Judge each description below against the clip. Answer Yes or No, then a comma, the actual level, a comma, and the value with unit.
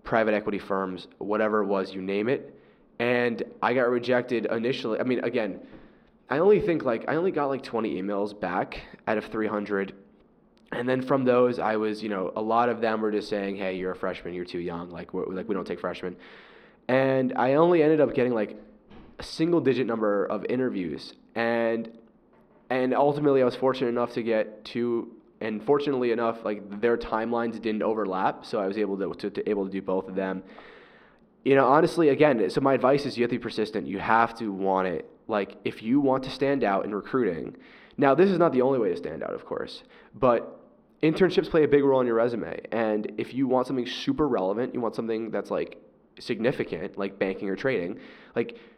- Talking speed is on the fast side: Yes, fast, 210 wpm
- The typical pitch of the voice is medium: No, low, 115 Hz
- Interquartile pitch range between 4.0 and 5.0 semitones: Yes, average, 4.3 semitones